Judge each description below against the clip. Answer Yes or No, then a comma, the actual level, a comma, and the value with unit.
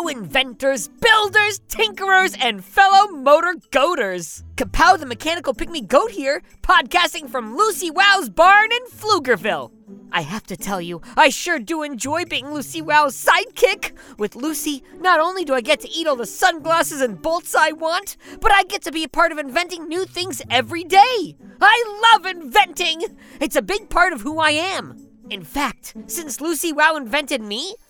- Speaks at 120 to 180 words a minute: Yes, average, 170 wpm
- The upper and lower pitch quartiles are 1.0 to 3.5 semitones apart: No, wide, 5.5 semitones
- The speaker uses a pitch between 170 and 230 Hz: No, very high, 320 Hz